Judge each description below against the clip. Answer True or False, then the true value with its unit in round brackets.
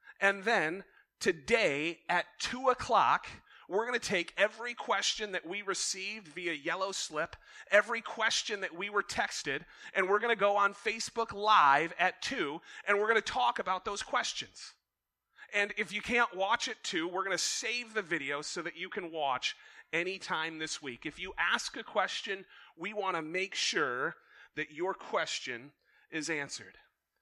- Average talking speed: True (170 wpm)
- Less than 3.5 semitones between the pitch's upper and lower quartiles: False (4.1 semitones)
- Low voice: False (195 Hz)